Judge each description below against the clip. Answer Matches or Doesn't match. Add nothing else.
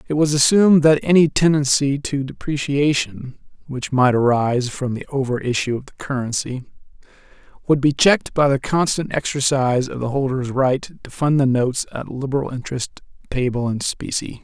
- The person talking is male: Matches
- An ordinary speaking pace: Matches